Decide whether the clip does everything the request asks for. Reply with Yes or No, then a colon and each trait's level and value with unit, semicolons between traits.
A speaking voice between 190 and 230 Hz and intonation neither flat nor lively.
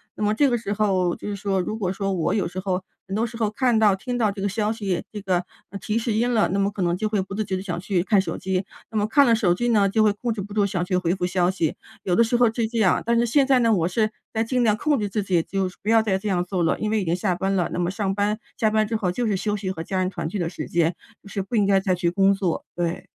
Yes: high, 200 Hz; average, 3.0 semitones